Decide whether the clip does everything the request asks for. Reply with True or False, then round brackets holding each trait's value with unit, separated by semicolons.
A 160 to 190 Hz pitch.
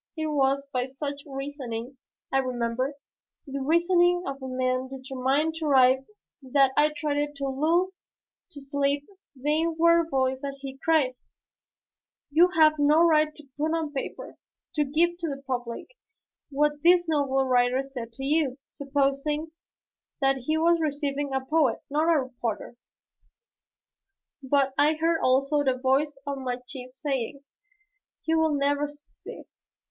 False (280 Hz)